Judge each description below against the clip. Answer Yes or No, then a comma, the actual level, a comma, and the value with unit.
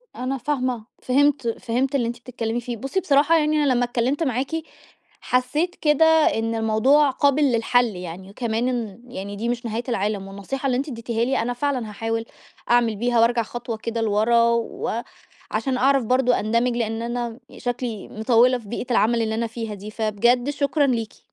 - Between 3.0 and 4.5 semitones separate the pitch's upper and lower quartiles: No, narrow, 2.6 semitones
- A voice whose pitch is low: No, high, 240 Hz